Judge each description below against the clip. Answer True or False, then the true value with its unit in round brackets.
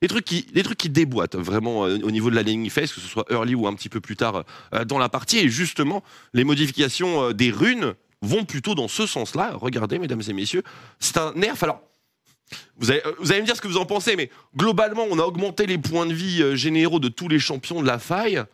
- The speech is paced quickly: True (240 wpm)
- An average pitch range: False (7.5 semitones)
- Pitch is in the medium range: True (155 Hz)